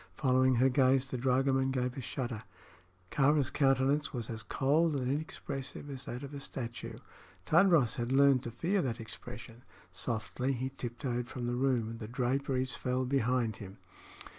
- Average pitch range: No, narrow, 2.2 semitones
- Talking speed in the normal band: Yes, average, 165 wpm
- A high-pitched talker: No, low, 130 Hz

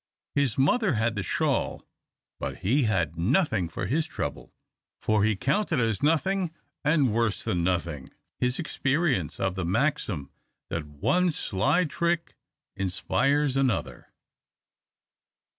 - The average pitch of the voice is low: Yes, low, 120 Hz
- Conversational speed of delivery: No, slow, 125 wpm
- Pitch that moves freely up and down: Yes, wide, 8.0 semitones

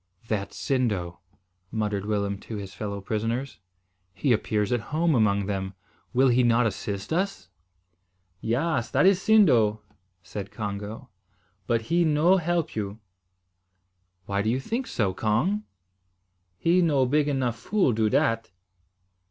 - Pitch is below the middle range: Yes, low, 115 Hz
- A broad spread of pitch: Yes, wide, 6.4 semitones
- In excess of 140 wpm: No, slow, 135 wpm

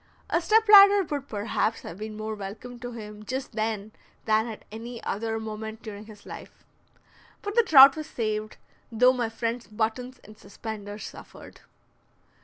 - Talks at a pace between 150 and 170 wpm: Yes, average, 160 wpm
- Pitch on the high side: Yes, high, 225 Hz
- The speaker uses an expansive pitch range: No, average, 2.9 semitones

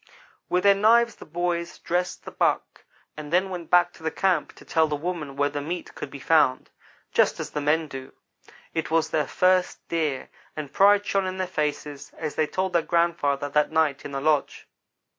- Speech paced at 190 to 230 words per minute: Yes, average, 200 wpm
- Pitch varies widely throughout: No, average, 3.5 semitones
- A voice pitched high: No, medium, 160 Hz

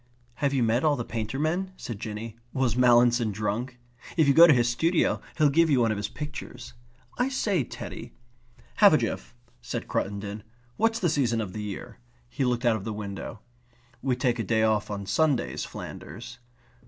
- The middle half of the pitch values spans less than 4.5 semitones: No, average, 5.1 semitones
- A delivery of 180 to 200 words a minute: Yes, average, 190 wpm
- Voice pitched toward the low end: Yes, low, 120 Hz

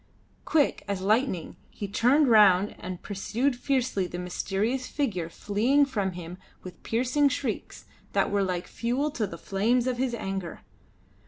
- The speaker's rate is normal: Yes, average, 150 wpm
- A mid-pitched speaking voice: No, high, 215 Hz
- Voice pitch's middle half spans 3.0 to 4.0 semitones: No, average, 5.0 semitones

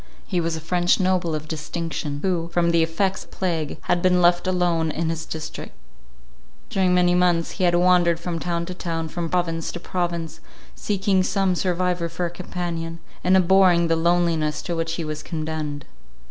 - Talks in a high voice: No, medium, 170 Hz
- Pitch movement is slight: Yes, narrow, 1.6 semitones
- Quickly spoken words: No, average, 180 wpm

